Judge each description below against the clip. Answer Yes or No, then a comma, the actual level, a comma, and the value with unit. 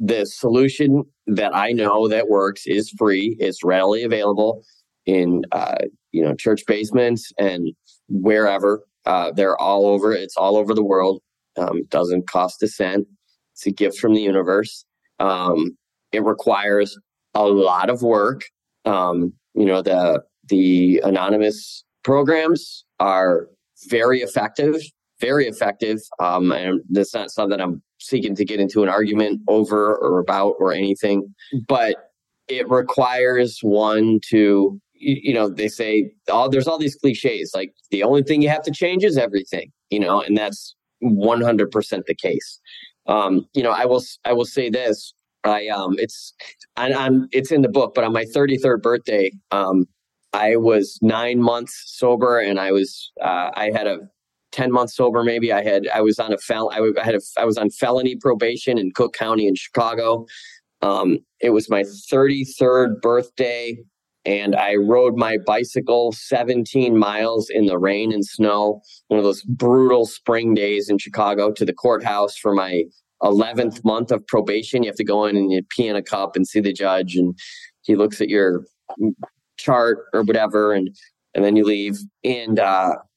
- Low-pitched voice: Yes, low, 110 Hz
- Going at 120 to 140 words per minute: No, average, 170 wpm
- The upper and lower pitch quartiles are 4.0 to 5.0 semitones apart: No, average, 3.5 semitones